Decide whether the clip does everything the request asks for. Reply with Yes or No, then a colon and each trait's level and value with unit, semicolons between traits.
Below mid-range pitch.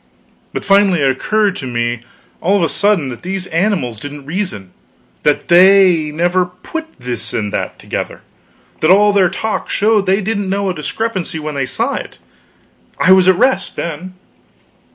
No: medium, 185 Hz